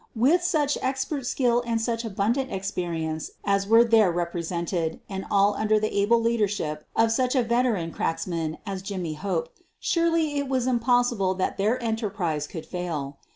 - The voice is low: No, high, 215 Hz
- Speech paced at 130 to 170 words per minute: Yes, average, 160 wpm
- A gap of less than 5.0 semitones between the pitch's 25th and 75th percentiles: No, wide, 5.5 semitones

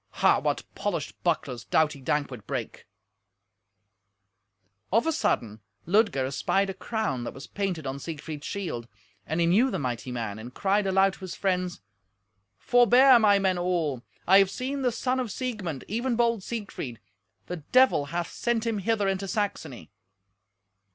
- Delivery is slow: No, average, 155 wpm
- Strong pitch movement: Yes, wide, 7.6 semitones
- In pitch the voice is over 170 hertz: Yes, high, 190 Hz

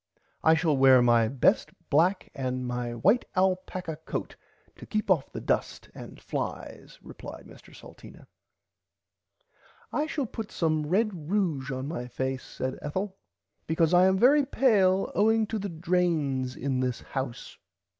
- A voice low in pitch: No, medium, 160 Hz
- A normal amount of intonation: No, wide, 6.7 semitones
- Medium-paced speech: Yes, average, 145 wpm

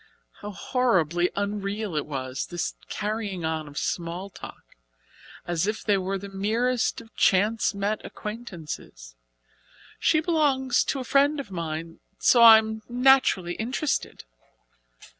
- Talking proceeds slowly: Yes, slow, 130 wpm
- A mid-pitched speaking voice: No, high, 205 Hz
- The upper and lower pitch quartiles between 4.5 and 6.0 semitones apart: Yes, average, 5.3 semitones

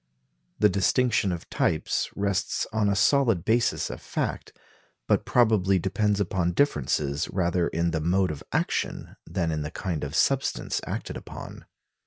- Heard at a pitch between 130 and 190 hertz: No, very low, 95 Hz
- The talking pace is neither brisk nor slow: Yes, average, 150 wpm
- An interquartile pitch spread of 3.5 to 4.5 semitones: Yes, average, 3.9 semitones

